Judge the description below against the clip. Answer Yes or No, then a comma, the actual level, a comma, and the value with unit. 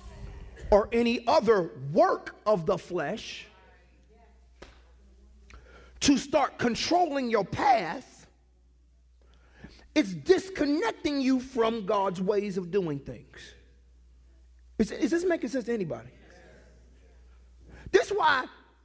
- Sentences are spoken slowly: Yes, slow, 100 wpm